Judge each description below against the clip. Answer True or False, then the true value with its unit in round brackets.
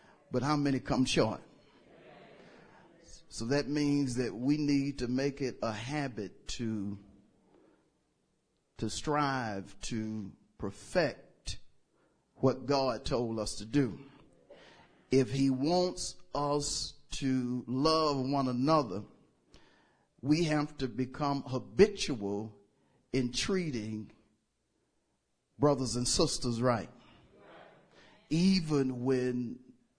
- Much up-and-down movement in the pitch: False (3.2 semitones)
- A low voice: True (130 Hz)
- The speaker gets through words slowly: True (95 wpm)